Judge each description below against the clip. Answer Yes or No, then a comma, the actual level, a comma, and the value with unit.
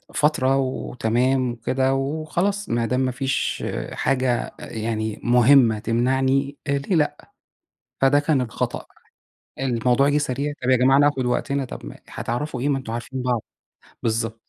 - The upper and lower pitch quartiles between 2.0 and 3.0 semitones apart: Yes, narrow, 2.5 semitones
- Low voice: Yes, low, 130 Hz